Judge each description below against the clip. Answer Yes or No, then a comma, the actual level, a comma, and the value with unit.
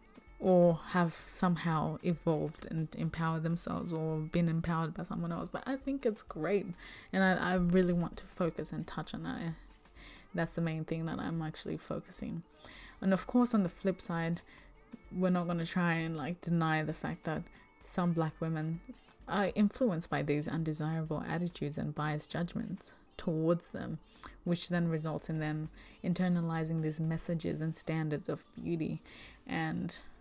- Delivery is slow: No, average, 165 wpm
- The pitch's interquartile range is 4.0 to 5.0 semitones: No, narrow, 2.4 semitones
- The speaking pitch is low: No, medium, 170 Hz